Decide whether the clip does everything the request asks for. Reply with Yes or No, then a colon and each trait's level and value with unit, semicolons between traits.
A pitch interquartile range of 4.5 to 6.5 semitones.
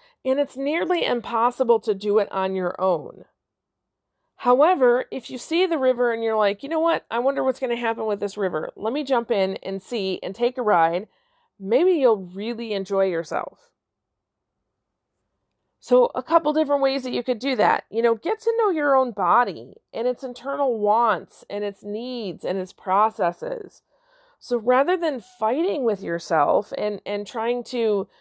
Yes: average, 4.9 semitones